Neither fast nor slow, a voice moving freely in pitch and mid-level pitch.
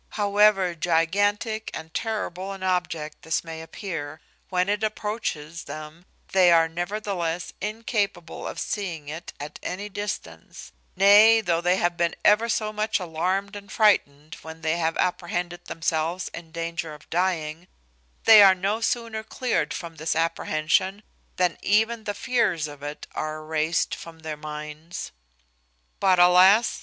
No: average, 145 wpm; average, 4.1 semitones; medium, 175 Hz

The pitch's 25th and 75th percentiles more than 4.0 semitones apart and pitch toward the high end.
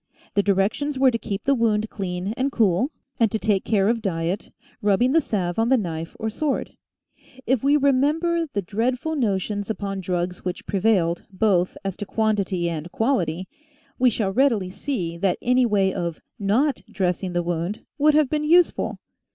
Yes: wide, 5.6 semitones; high, 210 Hz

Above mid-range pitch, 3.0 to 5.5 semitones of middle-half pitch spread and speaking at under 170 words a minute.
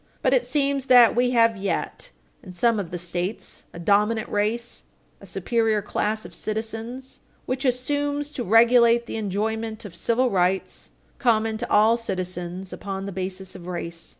Yes: high, 220 Hz; average, 3.8 semitones; average, 160 wpm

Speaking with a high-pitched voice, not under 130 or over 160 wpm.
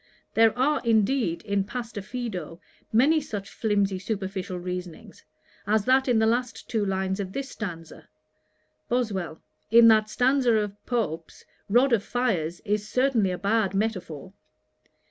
Yes: high, 215 Hz; average, 140 wpm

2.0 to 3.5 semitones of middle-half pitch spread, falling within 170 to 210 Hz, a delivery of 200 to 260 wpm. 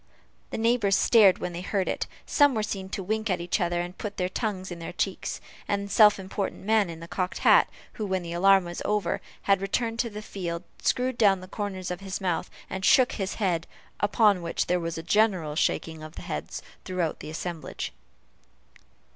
Yes: average, 3.1 semitones; high, 190 Hz; fast, 205 wpm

